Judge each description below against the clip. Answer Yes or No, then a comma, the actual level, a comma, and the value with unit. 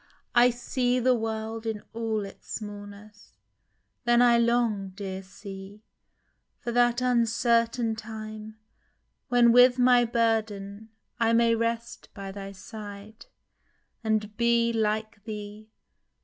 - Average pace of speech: No, slow, 115 wpm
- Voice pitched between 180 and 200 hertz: No, high, 225 Hz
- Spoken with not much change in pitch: Yes, narrow, 2.1 semitones